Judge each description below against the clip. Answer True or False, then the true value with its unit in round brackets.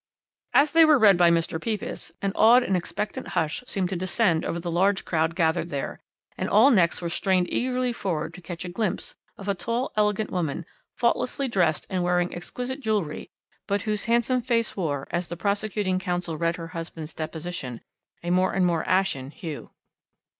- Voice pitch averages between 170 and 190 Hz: True (185 Hz)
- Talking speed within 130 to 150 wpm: False (180 wpm)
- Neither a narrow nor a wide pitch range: True (4.2 semitones)